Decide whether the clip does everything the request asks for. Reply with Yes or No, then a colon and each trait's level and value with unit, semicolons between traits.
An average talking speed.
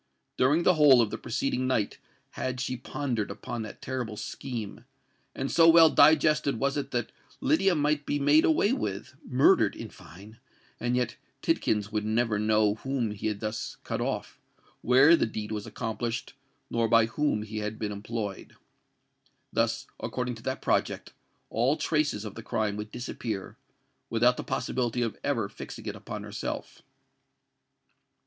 Yes: average, 155 wpm